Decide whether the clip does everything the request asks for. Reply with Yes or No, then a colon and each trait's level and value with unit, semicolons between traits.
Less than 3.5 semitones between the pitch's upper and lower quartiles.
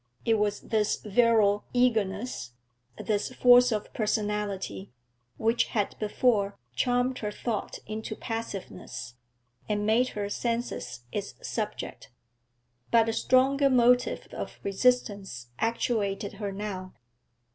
Yes: average, 3.1 semitones